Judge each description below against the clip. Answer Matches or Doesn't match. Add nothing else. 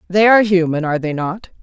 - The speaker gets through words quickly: Matches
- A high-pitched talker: Doesn't match